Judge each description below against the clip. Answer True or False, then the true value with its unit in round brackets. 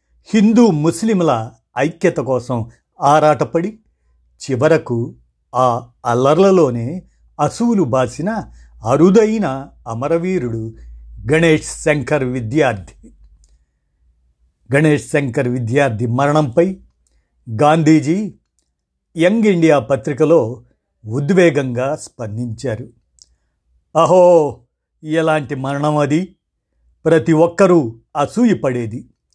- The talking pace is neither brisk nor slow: False (65 wpm)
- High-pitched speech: False (140 Hz)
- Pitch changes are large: True (6.4 semitones)